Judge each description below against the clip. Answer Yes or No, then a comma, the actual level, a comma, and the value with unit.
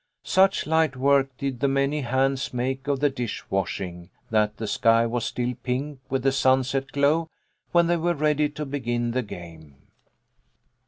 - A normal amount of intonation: Yes, average, 3.2 semitones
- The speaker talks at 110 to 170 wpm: Yes, average, 165 wpm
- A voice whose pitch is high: No, low, 135 Hz